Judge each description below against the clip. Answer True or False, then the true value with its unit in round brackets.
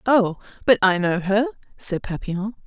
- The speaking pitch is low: False (205 Hz)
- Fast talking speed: False (160 wpm)